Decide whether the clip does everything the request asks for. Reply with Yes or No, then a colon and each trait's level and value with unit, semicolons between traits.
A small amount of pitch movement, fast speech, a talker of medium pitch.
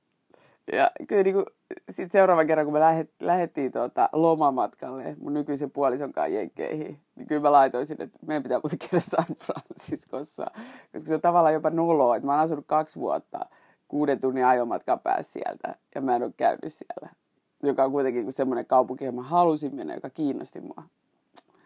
No: average, 3.5 semitones; fast, 170 wpm; medium, 150 Hz